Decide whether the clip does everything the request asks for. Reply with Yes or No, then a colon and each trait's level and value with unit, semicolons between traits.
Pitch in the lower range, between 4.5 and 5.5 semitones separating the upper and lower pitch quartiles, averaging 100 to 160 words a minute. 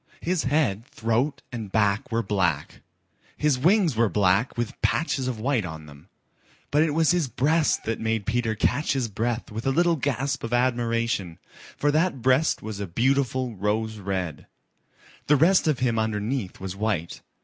No: low, 115 Hz; average, 5.1 semitones; average, 170 wpm